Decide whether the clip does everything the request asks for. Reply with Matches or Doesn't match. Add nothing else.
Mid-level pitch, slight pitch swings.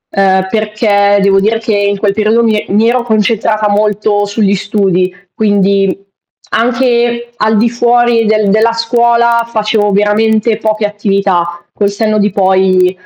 Doesn't match